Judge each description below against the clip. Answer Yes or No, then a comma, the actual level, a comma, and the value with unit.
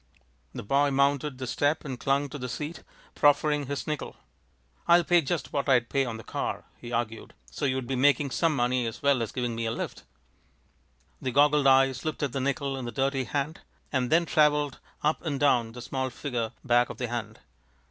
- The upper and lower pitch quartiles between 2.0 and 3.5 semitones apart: Yes, average, 2.8 semitones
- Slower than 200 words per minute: No, fast, 205 wpm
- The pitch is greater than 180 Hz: No, low, 135 Hz